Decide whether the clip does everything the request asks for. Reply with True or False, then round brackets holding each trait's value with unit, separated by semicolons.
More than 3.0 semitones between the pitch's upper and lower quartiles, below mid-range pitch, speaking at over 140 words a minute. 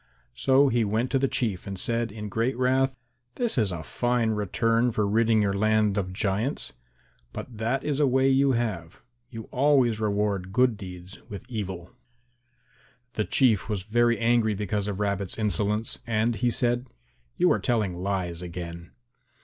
True (3.5 semitones; 110 Hz; 165 wpm)